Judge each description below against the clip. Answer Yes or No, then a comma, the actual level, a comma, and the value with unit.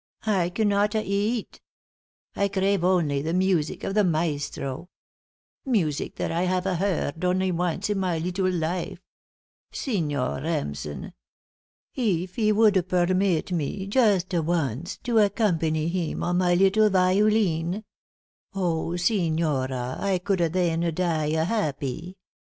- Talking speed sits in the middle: No, slow, 120 wpm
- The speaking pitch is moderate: Yes, medium, 180 Hz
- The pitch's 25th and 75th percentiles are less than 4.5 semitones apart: Yes, average, 3.4 semitones